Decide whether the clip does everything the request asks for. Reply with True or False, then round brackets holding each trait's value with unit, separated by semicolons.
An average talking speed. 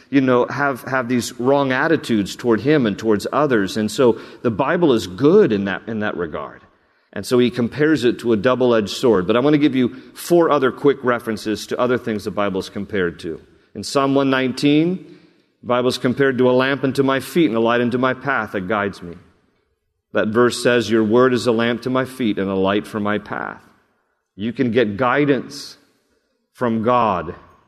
False (210 wpm)